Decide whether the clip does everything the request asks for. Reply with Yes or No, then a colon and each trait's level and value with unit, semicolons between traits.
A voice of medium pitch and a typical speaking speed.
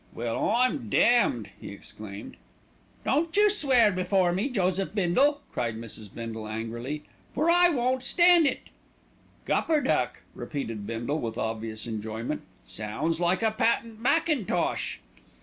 No: medium, 180 Hz; slow, 125 wpm